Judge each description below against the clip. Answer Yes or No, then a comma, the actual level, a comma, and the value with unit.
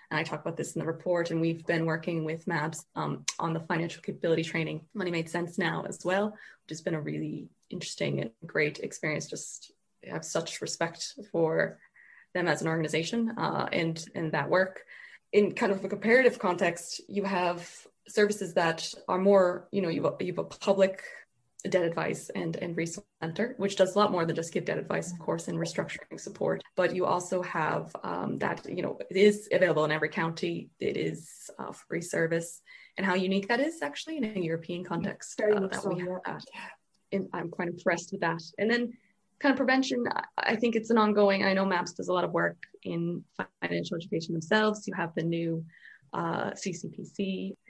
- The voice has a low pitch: No, medium, 180 Hz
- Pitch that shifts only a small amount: No, average, 3.4 semitones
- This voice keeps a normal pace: Yes, average, 195 wpm